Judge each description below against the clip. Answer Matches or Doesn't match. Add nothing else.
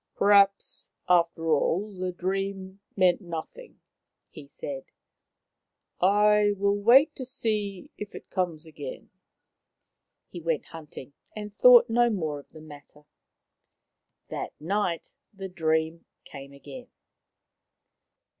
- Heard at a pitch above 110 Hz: Matches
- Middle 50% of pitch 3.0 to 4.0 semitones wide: Doesn't match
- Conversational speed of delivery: Doesn't match